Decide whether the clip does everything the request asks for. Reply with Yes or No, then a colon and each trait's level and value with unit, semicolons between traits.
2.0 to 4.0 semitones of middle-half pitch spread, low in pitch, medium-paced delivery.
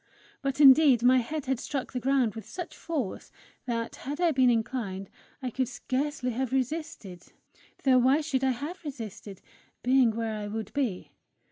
No: average, 3.3 semitones; very high, 255 Hz; average, 165 wpm